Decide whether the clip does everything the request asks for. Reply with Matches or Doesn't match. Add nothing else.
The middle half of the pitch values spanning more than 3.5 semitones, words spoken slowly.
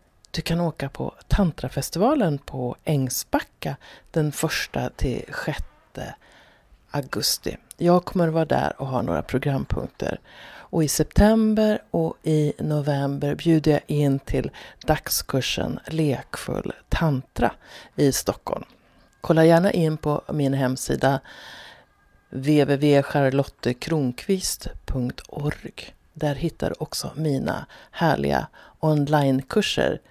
Doesn't match